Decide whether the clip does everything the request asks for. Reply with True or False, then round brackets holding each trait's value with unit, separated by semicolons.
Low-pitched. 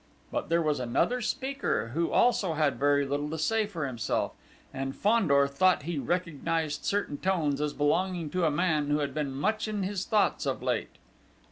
False (155 Hz)